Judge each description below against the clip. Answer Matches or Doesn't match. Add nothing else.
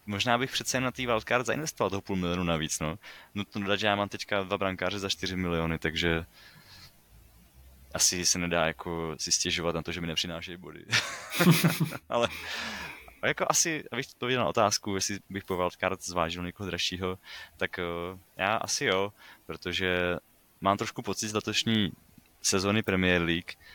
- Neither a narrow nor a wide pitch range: Matches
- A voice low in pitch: Matches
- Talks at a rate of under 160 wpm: Doesn't match